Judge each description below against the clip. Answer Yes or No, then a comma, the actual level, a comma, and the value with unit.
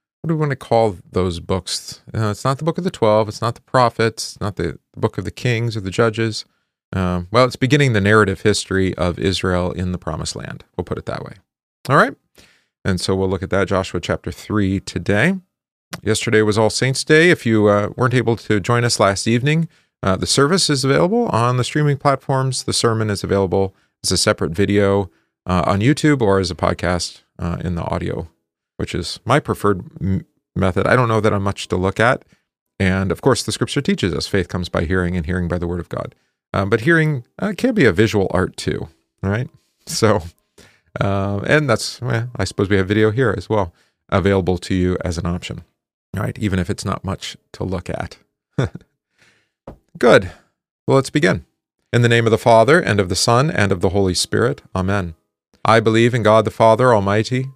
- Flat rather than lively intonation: No, average, 4.7 semitones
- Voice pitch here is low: Yes, low, 105 Hz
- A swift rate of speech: Yes, fast, 210 wpm